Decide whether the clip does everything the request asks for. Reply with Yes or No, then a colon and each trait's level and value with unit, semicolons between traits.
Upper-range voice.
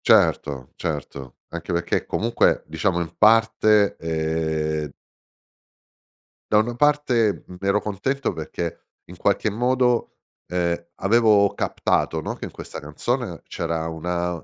No: very low, 90 Hz